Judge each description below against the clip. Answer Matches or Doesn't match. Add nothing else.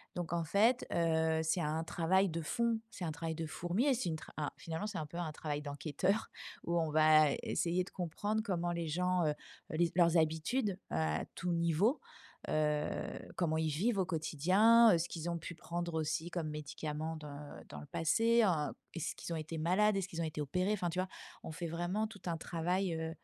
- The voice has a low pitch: Doesn't match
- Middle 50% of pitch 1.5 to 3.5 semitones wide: Matches